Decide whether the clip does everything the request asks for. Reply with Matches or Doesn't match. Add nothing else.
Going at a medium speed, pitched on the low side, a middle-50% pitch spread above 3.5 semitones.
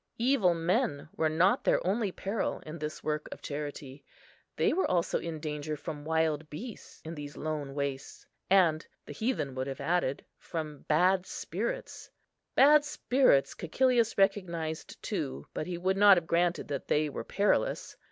Doesn't match